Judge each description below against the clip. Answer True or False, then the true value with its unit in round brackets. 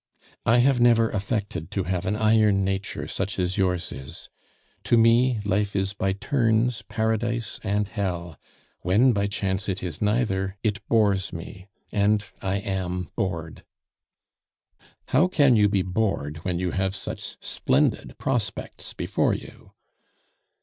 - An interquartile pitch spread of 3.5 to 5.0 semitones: False (2.9 semitones)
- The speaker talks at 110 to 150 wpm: True (145 wpm)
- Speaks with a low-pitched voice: True (100 Hz)